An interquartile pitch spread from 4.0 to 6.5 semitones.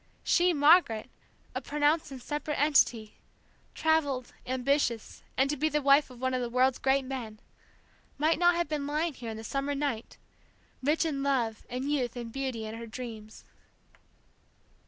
No: average, 3.5 semitones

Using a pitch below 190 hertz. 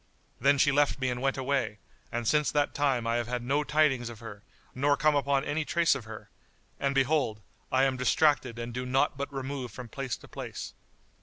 Yes: low, 135 Hz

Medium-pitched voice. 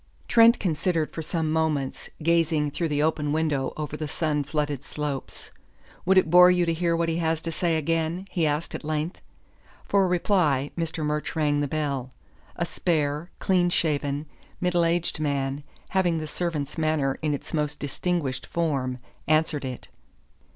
Yes: medium, 155 Hz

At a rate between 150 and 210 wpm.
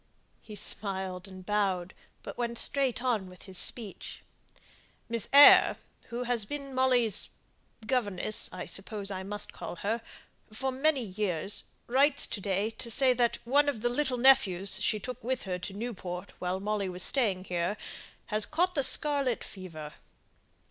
Yes: average, 155 wpm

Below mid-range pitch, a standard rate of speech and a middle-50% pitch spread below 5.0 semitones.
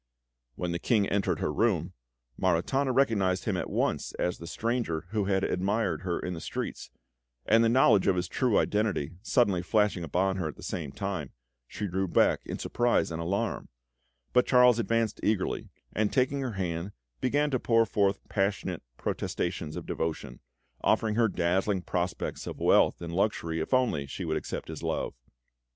Yes: low, 100 Hz; average, 170 wpm; average, 4.5 semitones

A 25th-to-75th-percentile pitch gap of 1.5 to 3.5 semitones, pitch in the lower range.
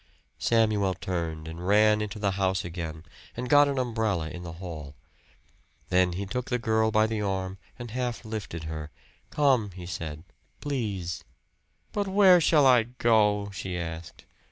No: average, 5.1 semitones; low, 100 Hz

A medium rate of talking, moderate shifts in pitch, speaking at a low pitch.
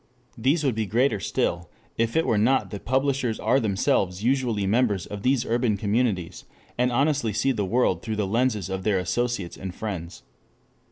Yes: average, 175 wpm; average, 4.3 semitones; low, 110 Hz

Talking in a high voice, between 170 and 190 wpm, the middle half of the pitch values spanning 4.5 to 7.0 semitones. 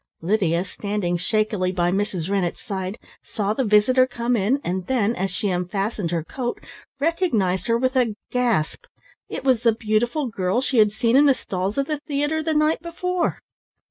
Yes: high, 215 Hz; average, 175 wpm; wide, 5.4 semitones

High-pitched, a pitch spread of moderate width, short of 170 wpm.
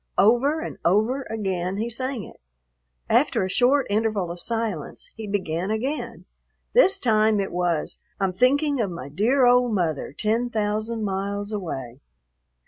Yes: high, 215 Hz; average, 4.4 semitones; average, 145 wpm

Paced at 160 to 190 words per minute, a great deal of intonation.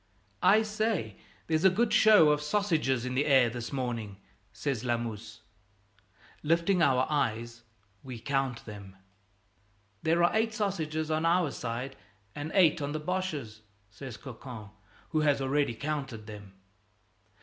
No: average, 140 wpm; wide, 5.9 semitones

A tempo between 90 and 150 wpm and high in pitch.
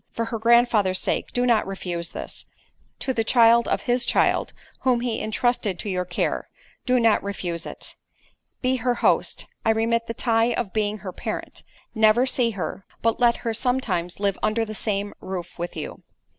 No: average, 170 wpm; high, 225 Hz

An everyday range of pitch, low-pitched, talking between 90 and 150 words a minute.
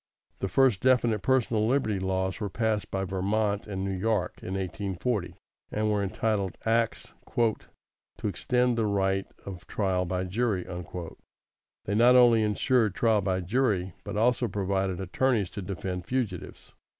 Yes: average, 3.3 semitones; low, 105 Hz; average, 140 wpm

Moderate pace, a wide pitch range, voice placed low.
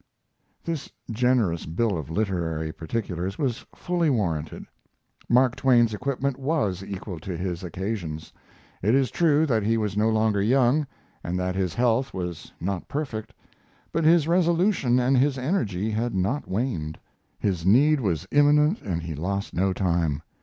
Yes: average, 150 wpm; wide, 6.8 semitones; low, 110 Hz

